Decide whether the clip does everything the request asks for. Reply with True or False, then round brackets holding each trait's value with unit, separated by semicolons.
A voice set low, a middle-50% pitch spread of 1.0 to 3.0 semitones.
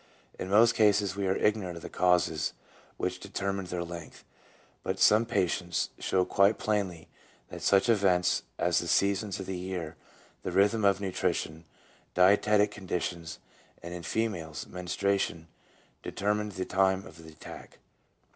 True (95 Hz; 2.4 semitones)